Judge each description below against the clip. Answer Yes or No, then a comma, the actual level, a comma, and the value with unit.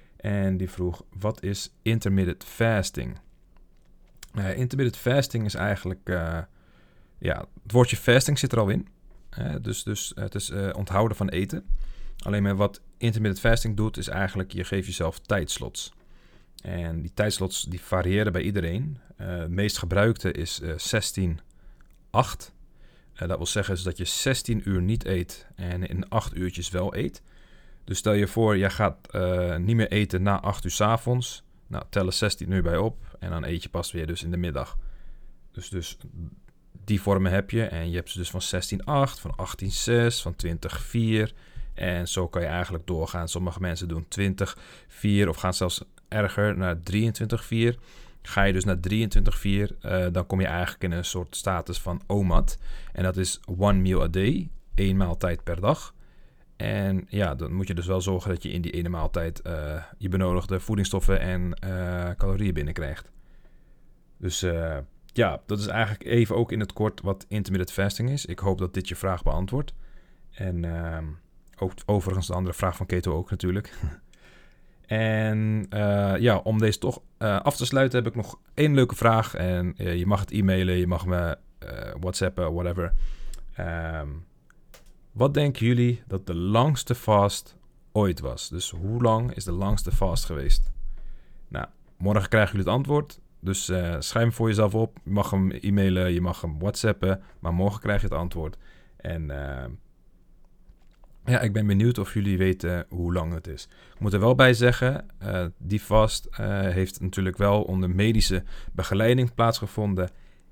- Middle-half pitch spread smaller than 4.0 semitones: Yes, average, 3.0 semitones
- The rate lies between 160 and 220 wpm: Yes, average, 175 wpm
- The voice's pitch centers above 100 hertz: No, very low, 95 Hz